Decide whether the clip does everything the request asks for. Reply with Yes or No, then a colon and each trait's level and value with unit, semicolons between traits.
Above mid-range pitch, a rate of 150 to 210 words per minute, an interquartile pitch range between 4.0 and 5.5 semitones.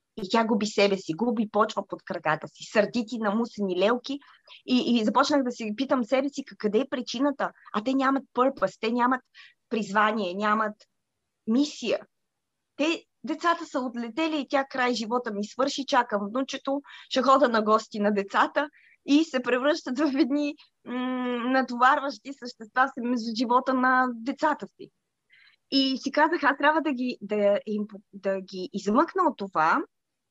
Yes: very high, 250 Hz; average, 160 wpm; average, 4.4 semitones